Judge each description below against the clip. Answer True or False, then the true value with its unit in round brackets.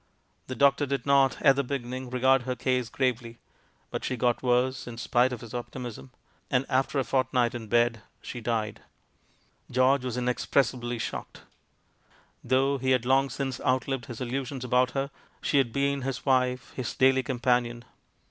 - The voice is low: True (125 Hz)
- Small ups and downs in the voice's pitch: True (1.6 semitones)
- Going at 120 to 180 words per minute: True (165 wpm)